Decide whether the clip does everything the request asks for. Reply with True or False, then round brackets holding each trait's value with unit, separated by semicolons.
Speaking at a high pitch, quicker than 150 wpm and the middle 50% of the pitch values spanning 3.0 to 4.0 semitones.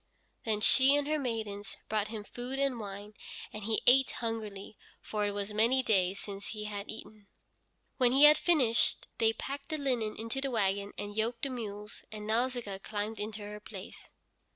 True (220 Hz; 180 wpm; 3.3 semitones)